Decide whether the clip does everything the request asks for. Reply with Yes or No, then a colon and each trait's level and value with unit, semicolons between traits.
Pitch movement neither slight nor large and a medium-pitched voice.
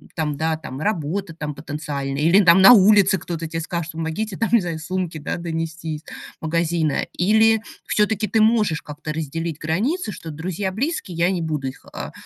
Yes: average, 3.9 semitones; medium, 165 Hz